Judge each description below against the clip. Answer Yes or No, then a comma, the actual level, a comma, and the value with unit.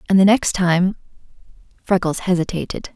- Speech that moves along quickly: No, slow, 120 wpm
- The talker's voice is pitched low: No, medium, 185 Hz